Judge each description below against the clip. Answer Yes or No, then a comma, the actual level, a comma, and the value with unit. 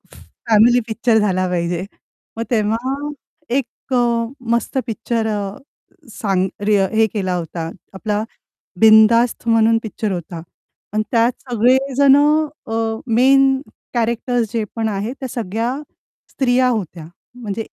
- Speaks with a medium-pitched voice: No, high, 225 Hz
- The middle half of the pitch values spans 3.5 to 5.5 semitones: No, average, 2.8 semitones